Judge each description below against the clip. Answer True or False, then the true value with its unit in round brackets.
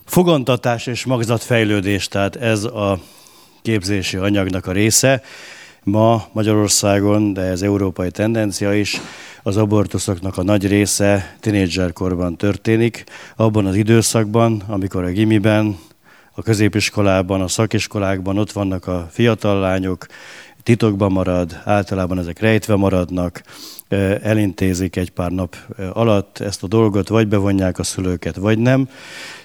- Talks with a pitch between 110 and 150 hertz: False (100 Hz)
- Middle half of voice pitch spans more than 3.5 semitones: False (2.7 semitones)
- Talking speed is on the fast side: False (120 wpm)